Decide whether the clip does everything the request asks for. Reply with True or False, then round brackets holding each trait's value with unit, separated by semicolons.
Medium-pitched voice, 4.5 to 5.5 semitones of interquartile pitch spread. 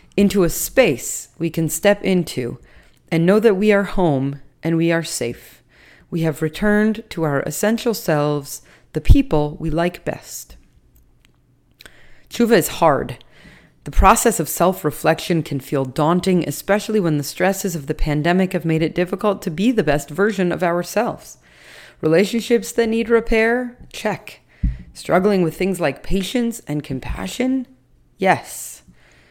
True (175 Hz; 5.1 semitones)